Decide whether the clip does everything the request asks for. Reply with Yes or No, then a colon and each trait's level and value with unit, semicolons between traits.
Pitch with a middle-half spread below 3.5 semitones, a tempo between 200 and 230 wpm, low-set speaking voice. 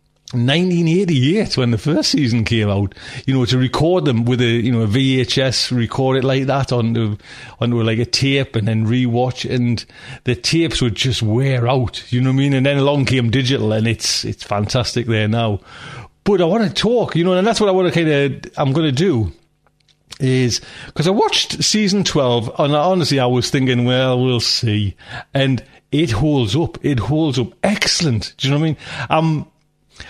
No: average, 4.3 semitones; fast, 205 wpm; low, 130 Hz